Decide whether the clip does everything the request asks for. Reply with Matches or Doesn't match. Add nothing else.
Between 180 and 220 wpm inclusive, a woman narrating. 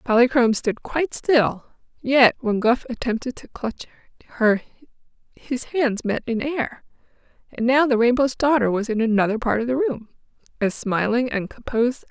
Doesn't match